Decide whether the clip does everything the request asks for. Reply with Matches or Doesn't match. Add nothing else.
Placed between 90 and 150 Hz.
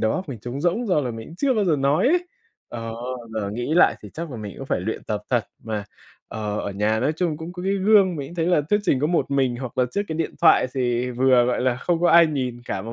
Matches